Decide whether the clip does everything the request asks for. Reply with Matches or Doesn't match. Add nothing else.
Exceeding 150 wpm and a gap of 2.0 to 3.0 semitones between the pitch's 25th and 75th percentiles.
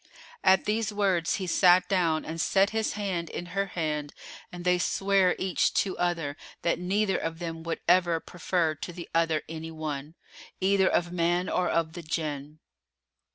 Matches